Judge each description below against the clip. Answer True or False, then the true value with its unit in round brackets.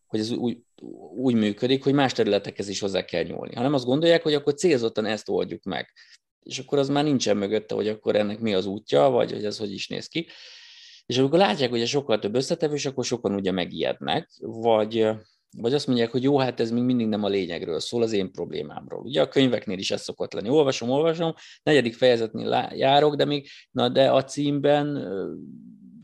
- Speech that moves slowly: False (205 wpm)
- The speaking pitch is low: True (125 Hz)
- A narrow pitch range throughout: False (5.0 semitones)